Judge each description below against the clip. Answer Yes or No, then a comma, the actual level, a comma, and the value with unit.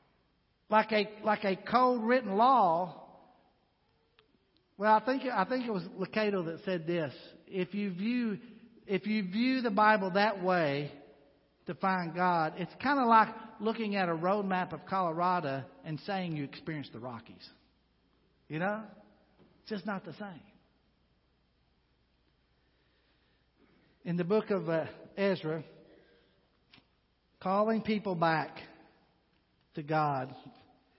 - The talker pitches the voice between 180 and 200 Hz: Yes, medium, 185 Hz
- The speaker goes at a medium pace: No, slow, 130 wpm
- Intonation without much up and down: No, wide, 5.6 semitones